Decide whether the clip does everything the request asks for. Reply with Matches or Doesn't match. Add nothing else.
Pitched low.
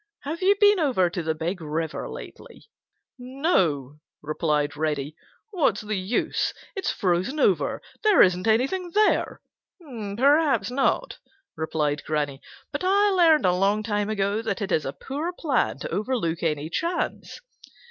Doesn't match